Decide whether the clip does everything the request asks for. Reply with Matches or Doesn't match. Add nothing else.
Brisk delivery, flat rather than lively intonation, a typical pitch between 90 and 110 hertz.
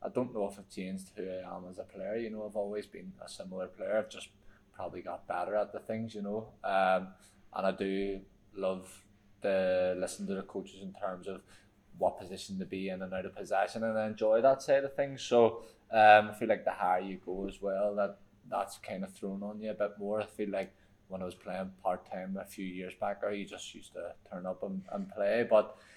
Matches